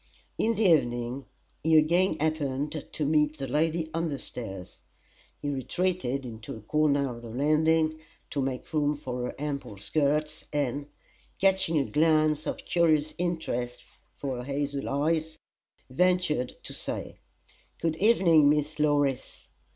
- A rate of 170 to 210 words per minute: No, average, 145 wpm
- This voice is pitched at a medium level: Yes, medium, 150 Hz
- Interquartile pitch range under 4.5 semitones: Yes, average, 2.9 semitones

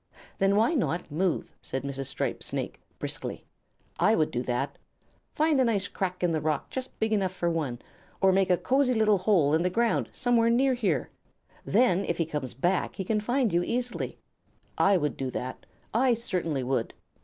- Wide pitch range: Yes, wide, 6.8 semitones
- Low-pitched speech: No, high, 190 Hz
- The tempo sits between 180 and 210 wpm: Yes, average, 190 wpm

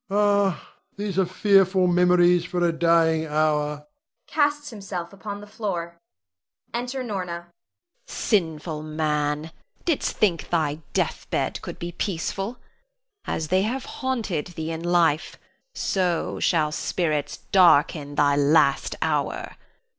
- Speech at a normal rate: No, slow, 125 wpm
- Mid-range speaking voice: Yes, medium, 175 Hz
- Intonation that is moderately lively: Yes, average, 4.0 semitones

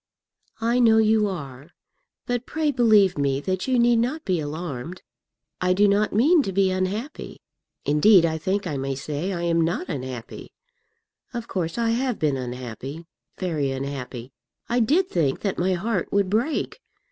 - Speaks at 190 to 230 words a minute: No, average, 165 wpm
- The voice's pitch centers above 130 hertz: Yes, medium, 185 Hz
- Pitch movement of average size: No, wide, 7.4 semitones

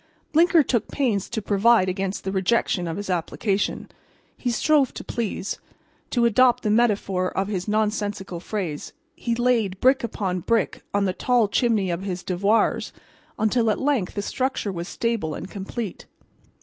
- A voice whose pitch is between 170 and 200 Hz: No, high, 210 Hz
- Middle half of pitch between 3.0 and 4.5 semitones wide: Yes, average, 3.8 semitones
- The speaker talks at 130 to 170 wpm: Yes, average, 160 wpm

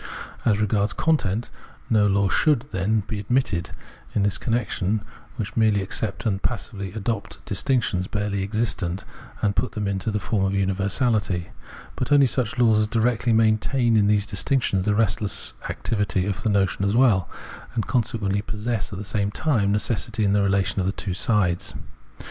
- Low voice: Yes, low, 105 Hz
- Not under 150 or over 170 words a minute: Yes, average, 165 wpm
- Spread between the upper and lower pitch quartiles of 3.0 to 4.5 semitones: No, narrow, 2.4 semitones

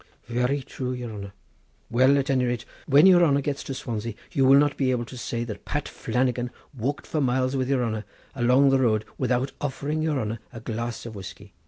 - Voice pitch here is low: Yes, low, 125 Hz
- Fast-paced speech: Yes, fast, 210 wpm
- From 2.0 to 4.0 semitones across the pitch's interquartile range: Yes, average, 2.8 semitones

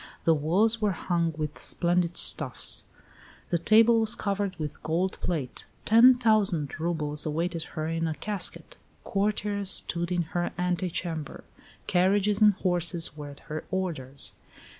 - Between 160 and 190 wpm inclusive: No, average, 140 wpm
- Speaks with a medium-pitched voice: Yes, medium, 175 Hz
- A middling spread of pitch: Yes, average, 4.0 semitones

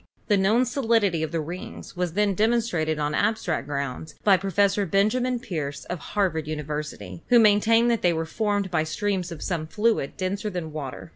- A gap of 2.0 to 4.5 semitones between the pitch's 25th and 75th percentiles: No, average, 5.1 semitones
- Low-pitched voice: No, medium, 185 Hz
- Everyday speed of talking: Yes, average, 185 wpm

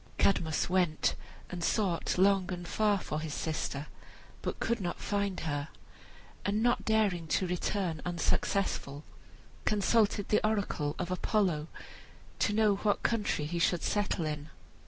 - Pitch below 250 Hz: Yes, medium, 185 Hz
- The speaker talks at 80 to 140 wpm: Yes, slow, 135 wpm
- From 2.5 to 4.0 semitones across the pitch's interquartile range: No, average, 4.4 semitones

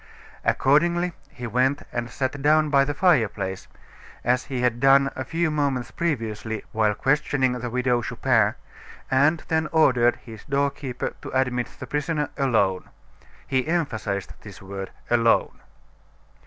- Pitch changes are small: No, average, 3.8 semitones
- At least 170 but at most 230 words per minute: No, average, 140 wpm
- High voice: No, low, 130 Hz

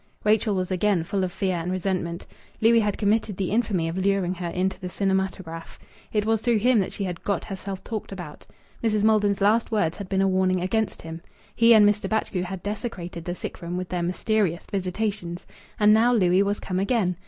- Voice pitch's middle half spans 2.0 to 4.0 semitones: Yes, average, 2.8 semitones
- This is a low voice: No, high, 195 Hz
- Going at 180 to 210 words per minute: Yes, fast, 205 wpm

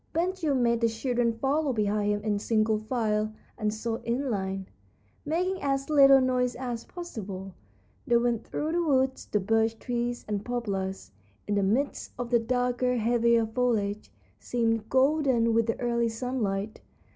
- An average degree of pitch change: Yes, average, 3.1 semitones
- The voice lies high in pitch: Yes, high, 235 Hz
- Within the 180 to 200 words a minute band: No, average, 155 wpm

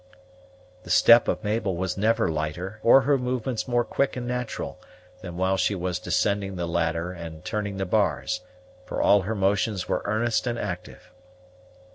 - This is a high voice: No, low, 100 Hz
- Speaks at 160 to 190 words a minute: Yes, average, 165 wpm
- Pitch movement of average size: Yes, average, 4.2 semitones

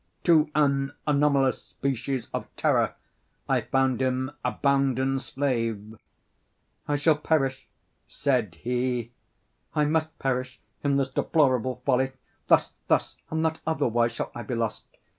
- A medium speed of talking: No, slow, 130 wpm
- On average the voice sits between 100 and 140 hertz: Yes, low, 135 Hz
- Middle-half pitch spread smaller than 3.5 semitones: Yes, narrow, 2.5 semitones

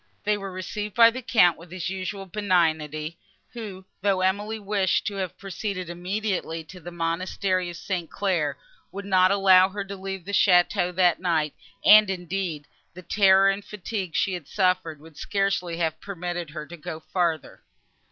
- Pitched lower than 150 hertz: No, medium, 185 Hz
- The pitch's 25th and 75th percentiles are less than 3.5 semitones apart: Yes, narrow, 2.5 semitones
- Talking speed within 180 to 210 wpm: No, average, 170 wpm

